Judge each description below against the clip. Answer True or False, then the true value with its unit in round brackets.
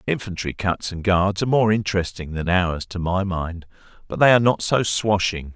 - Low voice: True (95 Hz)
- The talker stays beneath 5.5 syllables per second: True (5.2 syllables/s)